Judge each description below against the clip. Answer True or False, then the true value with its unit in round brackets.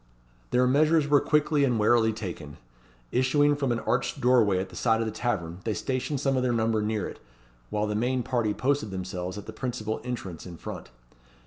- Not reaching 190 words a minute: False (200 wpm)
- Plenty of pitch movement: False (3.7 semitones)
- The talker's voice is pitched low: True (115 Hz)